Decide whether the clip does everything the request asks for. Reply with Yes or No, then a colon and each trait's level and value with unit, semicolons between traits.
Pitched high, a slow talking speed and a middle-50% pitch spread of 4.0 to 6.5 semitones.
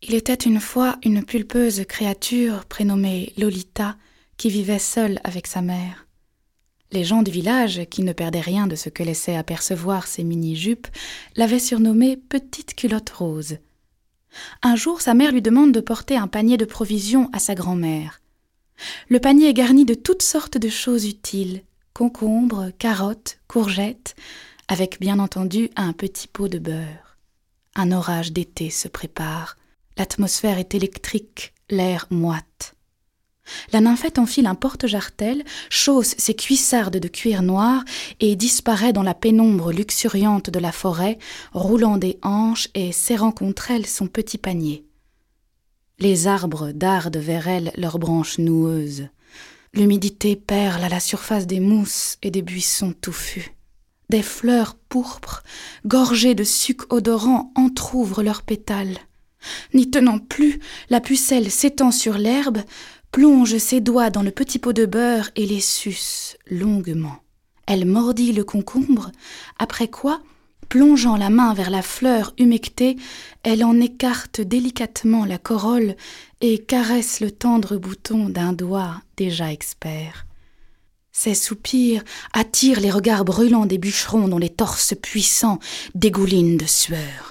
Yes: high, 210 Hz; slow, 140 wpm; average, 4.5 semitones